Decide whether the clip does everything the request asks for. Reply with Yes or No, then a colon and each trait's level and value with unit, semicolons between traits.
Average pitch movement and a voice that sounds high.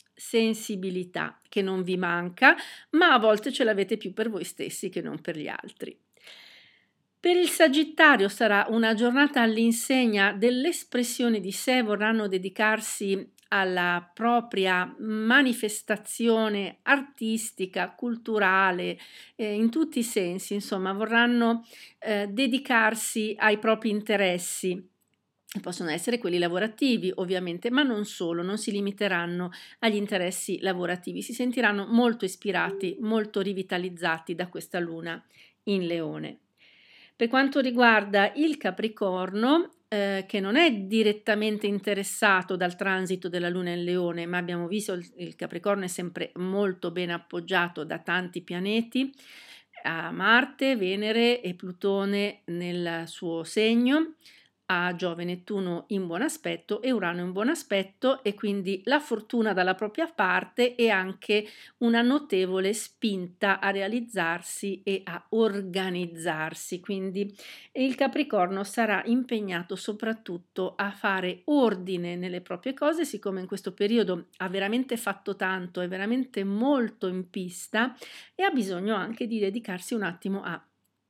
Yes: average, 3.9 semitones; high, 205 Hz